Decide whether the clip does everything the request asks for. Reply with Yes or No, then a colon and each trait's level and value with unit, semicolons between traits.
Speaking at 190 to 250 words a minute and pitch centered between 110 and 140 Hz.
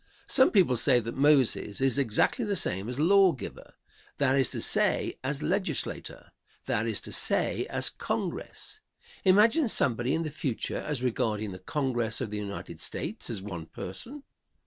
No: average, 165 wpm; low, 135 Hz